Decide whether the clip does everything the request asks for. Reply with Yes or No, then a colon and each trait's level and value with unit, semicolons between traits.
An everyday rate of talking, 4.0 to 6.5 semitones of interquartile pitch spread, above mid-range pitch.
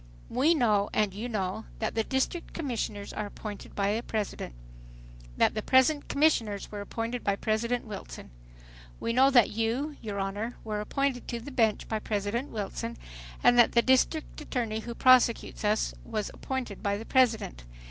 No: average, 170 wpm; average, 3.5 semitones; high, 225 Hz